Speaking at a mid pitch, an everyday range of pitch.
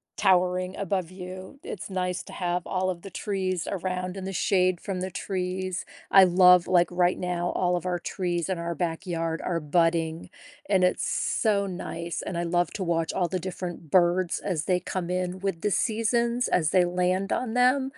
No: medium, 180 Hz; narrow, 1.4 semitones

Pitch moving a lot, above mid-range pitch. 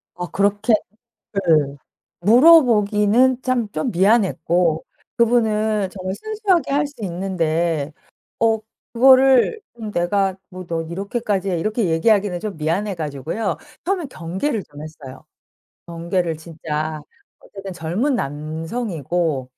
Yes: wide, 5.7 semitones; high, 195 Hz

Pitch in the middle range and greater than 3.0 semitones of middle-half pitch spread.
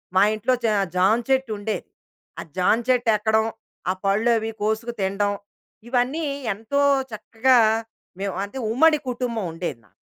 No: high, 220 Hz; average, 3.4 semitones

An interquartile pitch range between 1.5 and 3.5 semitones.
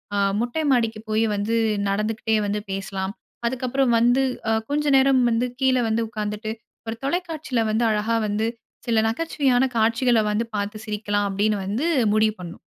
Yes: average, 3.1 semitones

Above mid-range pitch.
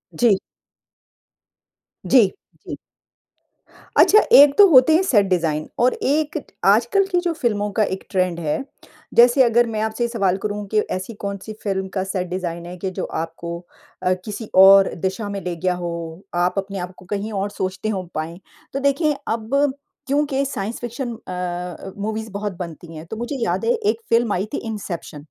Yes: high, 200 Hz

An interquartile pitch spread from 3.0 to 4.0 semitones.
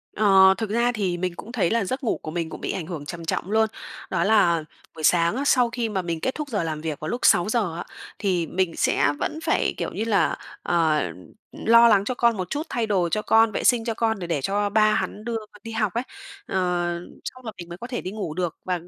No: average, 4.8 semitones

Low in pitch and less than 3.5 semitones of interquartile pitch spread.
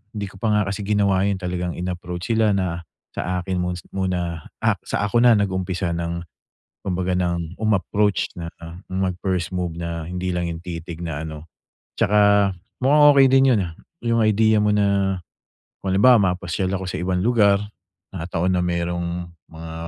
Yes: very low, 95 Hz; average, 2.7 semitones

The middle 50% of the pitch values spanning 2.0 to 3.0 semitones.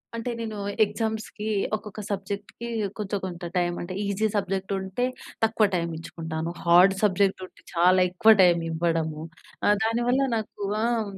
No: average, 3.8 semitones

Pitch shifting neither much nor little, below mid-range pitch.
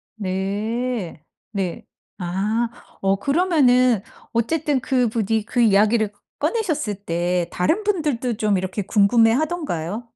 No: average, 4.6 semitones; high, 225 Hz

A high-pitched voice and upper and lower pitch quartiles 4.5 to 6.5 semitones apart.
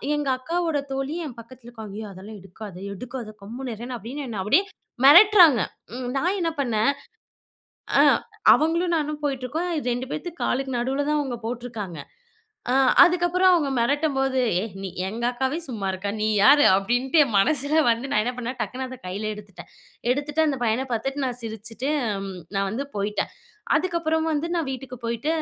Yes: very high, 255 Hz; average, 4.9 semitones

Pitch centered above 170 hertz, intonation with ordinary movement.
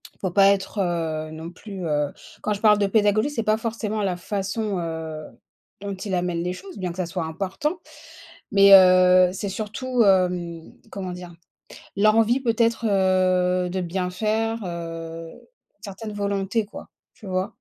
Yes: high, 190 Hz; average, 3.1 semitones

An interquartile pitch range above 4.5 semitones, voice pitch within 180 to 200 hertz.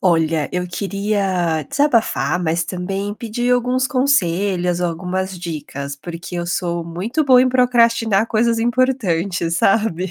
Yes: average, 5.3 semitones; high, 190 Hz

